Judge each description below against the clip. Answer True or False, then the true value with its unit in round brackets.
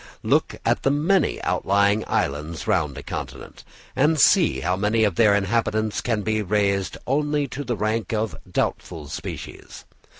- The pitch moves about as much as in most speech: True (3.7 semitones)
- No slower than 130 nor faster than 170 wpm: True (155 wpm)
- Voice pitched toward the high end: False (110 Hz)